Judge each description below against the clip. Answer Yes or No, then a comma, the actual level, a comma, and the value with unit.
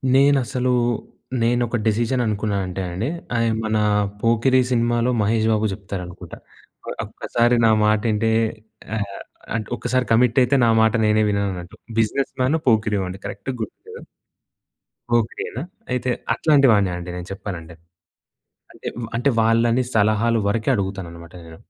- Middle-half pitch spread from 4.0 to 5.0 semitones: No, average, 3.0 semitones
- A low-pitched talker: Yes, low, 110 Hz